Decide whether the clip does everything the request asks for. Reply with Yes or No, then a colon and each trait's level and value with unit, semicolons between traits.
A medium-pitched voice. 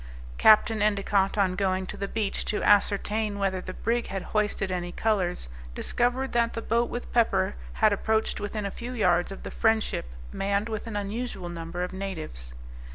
No: high, 200 Hz